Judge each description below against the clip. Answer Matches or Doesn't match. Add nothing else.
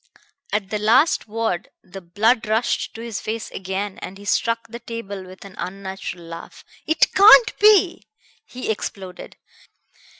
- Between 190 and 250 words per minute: Doesn't match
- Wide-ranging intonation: Doesn't match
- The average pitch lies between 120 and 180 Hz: Doesn't match